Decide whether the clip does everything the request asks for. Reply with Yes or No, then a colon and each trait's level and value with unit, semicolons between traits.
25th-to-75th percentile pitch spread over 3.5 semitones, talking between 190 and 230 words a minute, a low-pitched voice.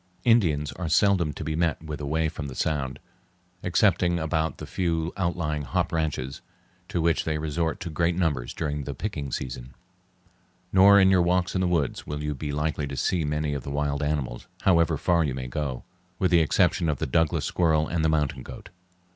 No: average, 3.0 semitones; average, 195 wpm; very low, 80 Hz